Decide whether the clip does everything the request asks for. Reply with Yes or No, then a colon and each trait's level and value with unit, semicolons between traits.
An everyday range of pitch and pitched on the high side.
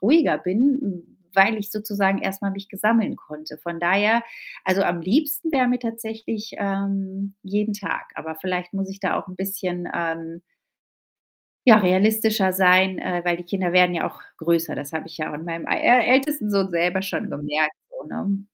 Yes: average, 3.3 semitones; high, 195 Hz